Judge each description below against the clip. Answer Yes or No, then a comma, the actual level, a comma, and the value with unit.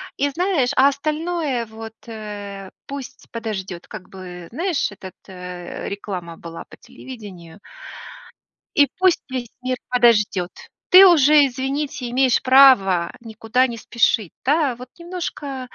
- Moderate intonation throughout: No, wide, 6.0 semitones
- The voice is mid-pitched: No, high, 245 Hz